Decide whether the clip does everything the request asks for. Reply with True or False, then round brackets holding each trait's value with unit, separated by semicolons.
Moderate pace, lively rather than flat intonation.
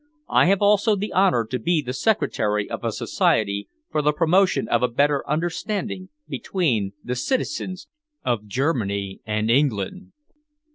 True (145 wpm; 9.0 semitones)